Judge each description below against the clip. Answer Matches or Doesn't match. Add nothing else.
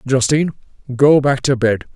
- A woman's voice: Doesn't match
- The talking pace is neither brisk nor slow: Matches